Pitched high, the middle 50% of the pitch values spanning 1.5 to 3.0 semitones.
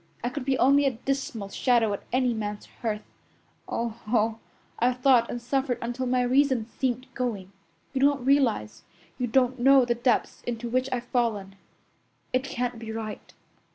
Yes: high, 245 Hz; narrow, 2.5 semitones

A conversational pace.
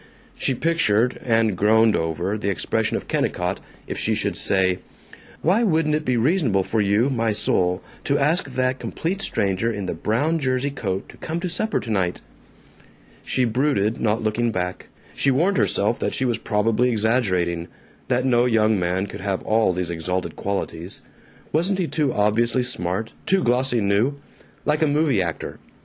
Yes: average, 165 wpm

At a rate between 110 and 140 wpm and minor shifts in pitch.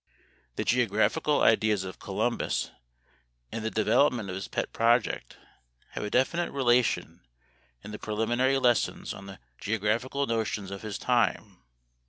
No: slow, 135 wpm; average, 3.1 semitones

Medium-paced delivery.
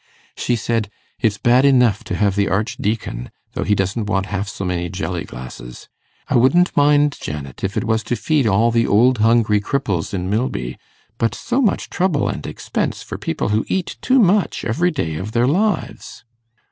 Yes: average, 185 wpm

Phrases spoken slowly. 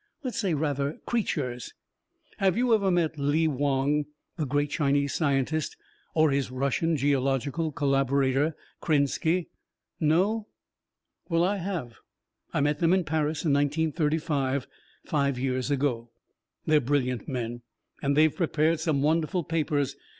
Yes: slow, 130 wpm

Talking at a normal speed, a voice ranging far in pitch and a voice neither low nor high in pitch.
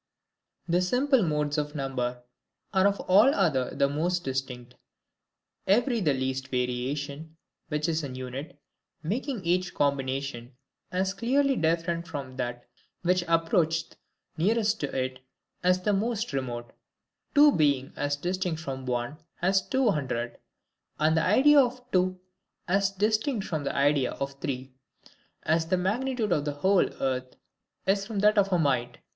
Yes: average, 145 wpm; wide, 6.4 semitones; medium, 160 Hz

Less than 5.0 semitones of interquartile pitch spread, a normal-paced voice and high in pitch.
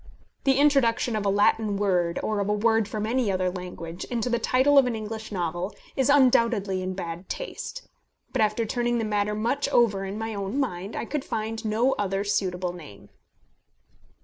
Yes: average, 3.6 semitones; average, 185 wpm; high, 215 Hz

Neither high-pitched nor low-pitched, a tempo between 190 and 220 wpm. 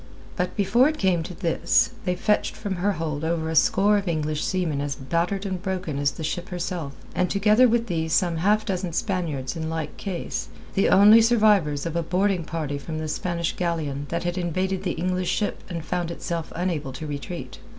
Yes: medium, 175 Hz; average, 200 wpm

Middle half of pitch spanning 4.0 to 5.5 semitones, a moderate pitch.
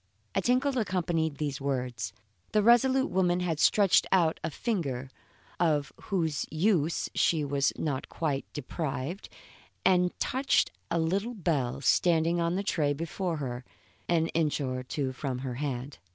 Yes: average, 4.7 semitones; medium, 160 Hz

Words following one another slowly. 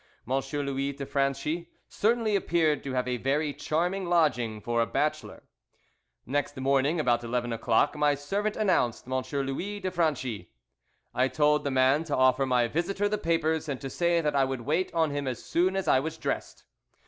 No: average, 185 wpm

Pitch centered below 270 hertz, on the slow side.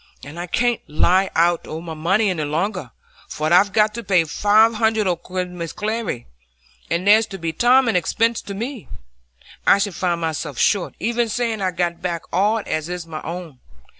No: medium, 185 Hz; average, 185 wpm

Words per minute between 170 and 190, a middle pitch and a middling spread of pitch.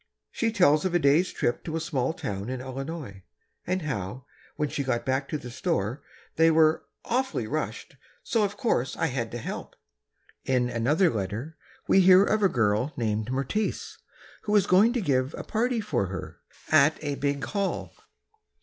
No: average, 175 wpm; medium, 145 Hz; wide, 7.0 semitones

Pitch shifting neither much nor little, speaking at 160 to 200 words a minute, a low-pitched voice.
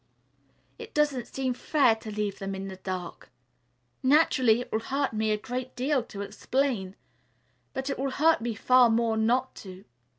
No: average, 4.0 semitones; average, 170 wpm; high, 240 Hz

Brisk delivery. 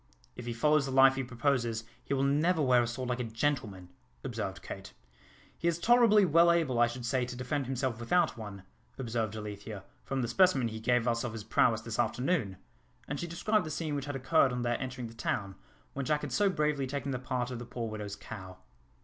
Yes: fast, 220 wpm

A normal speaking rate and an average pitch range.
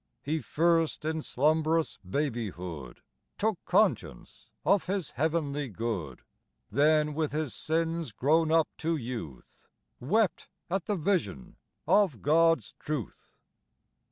No: slow, 110 wpm; average, 4.9 semitones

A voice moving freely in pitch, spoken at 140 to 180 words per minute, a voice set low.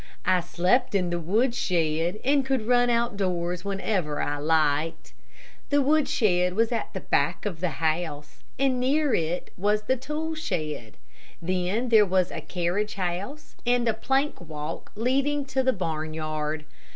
No: wide, 7.0 semitones; average, 150 wpm; high, 190 Hz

